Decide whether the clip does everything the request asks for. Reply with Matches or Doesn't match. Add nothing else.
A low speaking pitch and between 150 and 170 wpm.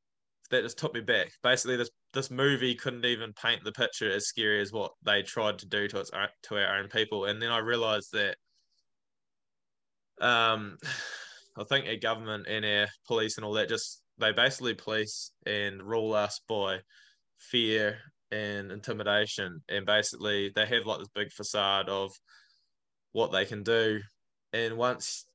Matches